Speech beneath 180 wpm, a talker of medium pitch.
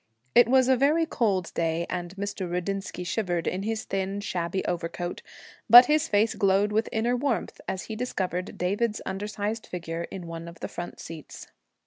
No: average, 170 wpm; high, 195 Hz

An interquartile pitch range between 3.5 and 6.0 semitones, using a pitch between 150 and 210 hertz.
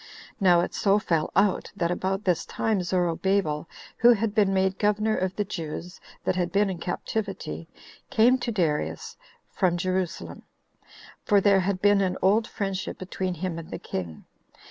No: narrow, 2.6 semitones; high, 190 Hz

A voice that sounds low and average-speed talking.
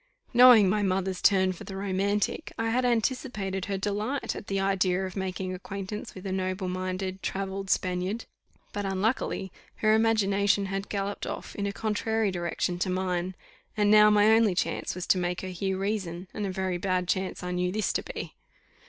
No: high, 195 Hz; average, 185 wpm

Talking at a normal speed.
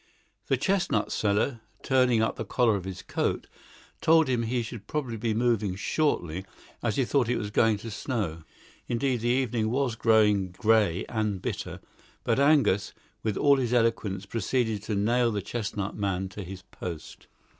Yes: average, 165 wpm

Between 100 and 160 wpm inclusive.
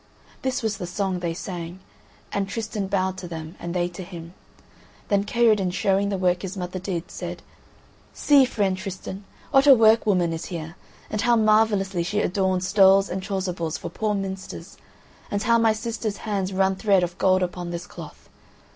No: average, 180 wpm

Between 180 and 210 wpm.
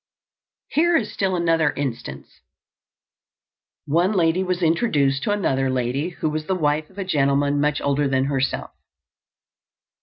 No: average, 140 wpm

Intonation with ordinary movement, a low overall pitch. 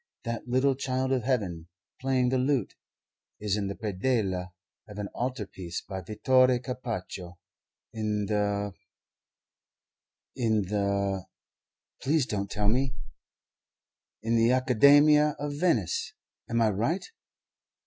Yes: average, 4.4 semitones; low, 115 Hz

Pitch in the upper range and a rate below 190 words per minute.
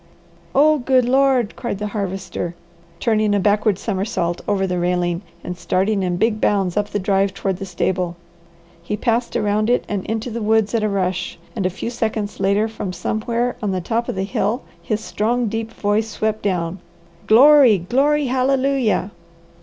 Yes: high, 210 Hz; average, 175 wpm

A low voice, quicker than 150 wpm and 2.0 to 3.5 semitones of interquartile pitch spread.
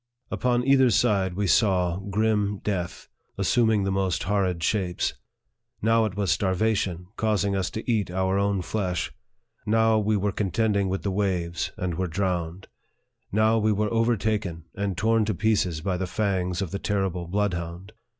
Yes: low, 100 Hz; average, 160 wpm; average, 2.9 semitones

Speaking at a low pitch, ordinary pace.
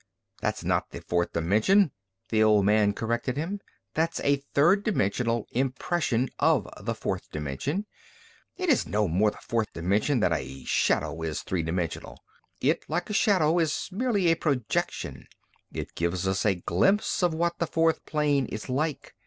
Yes: low, 125 Hz; average, 160 wpm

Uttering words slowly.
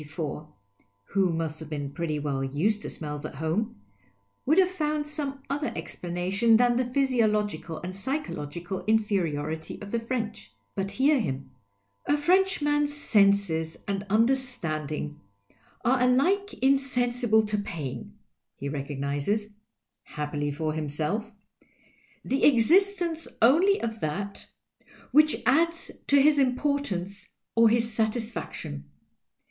Yes: slow, 125 wpm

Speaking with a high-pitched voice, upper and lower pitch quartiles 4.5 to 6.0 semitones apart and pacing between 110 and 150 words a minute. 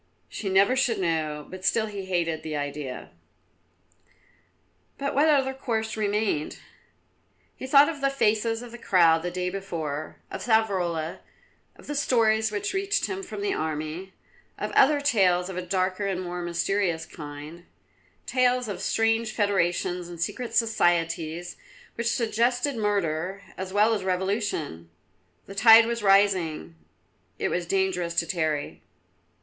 Yes: high, 195 Hz; average, 4.9 semitones; average, 145 wpm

